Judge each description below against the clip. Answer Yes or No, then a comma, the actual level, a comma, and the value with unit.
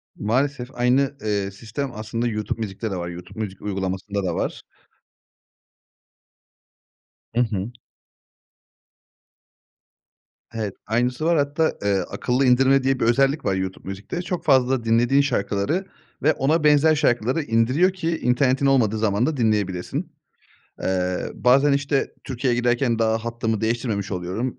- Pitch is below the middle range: Yes, low, 120 Hz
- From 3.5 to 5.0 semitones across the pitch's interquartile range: Yes, average, 4.7 semitones